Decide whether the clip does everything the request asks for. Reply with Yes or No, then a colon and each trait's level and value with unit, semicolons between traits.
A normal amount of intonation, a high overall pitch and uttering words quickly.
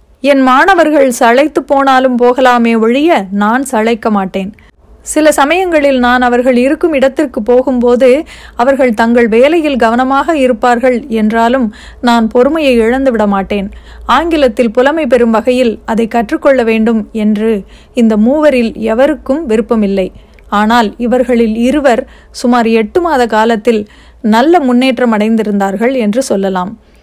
No: average, 3.0 semitones; high, 245 Hz; average, 110 wpm